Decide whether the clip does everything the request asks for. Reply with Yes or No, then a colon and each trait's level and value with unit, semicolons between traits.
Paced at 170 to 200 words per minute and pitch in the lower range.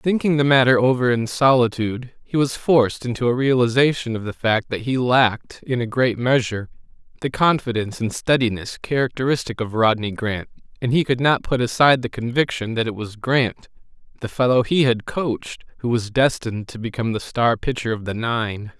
Yes: average, 185 wpm; low, 120 Hz